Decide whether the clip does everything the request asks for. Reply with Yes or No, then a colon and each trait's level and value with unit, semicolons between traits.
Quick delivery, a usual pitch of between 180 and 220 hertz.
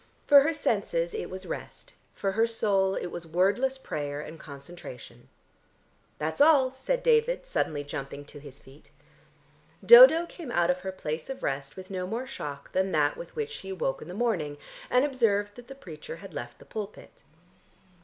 No: average, 180 wpm; high, 190 Hz